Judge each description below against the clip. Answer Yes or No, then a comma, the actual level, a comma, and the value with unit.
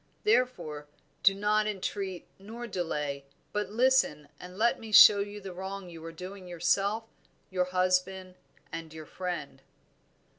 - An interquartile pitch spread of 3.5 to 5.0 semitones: No, average, 3.1 semitones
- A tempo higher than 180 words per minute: No, average, 140 wpm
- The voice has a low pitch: No, medium, 185 Hz